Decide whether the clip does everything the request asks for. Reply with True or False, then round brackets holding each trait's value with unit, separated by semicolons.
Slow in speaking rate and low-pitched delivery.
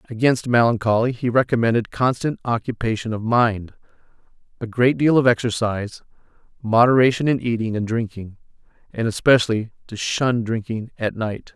True (130 wpm; 115 Hz)